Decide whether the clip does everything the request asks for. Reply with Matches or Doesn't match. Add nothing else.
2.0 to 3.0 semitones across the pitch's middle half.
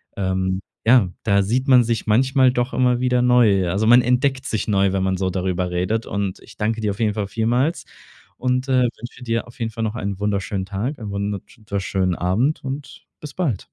Doesn't match